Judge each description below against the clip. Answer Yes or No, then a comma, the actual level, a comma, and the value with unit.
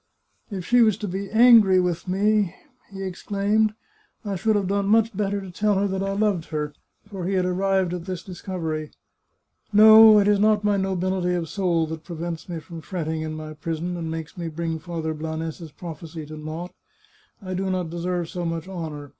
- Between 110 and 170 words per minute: No, fast, 205 wpm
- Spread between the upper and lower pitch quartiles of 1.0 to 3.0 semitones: No, average, 3.5 semitones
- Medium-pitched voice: Yes, medium, 180 Hz